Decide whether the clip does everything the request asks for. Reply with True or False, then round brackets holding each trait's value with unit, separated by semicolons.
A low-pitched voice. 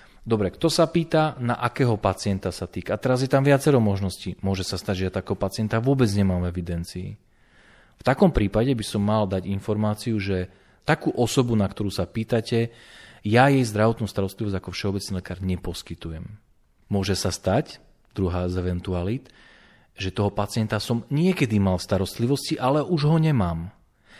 True (105 Hz)